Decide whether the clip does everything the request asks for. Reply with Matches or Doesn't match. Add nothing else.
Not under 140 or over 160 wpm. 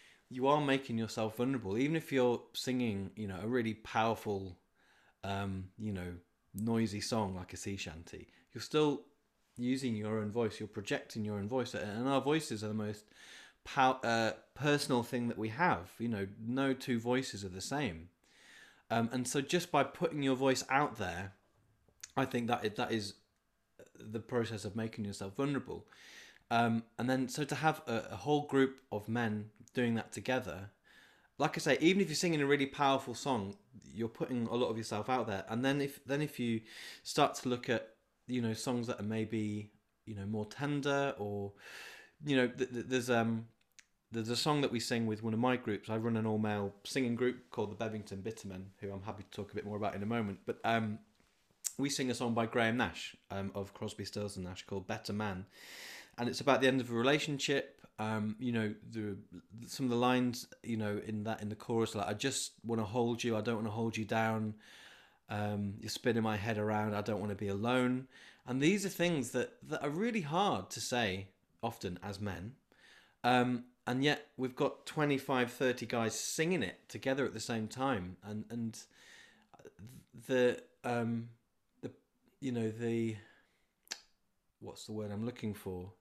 Doesn't match